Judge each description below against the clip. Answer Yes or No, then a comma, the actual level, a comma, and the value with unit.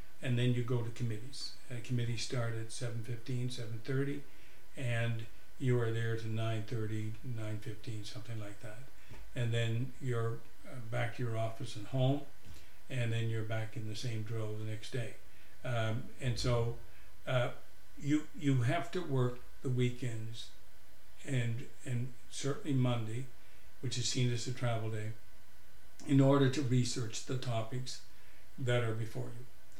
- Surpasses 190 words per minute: No, average, 150 wpm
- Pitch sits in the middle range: No, low, 115 Hz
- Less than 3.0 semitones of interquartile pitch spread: Yes, narrow, 2.5 semitones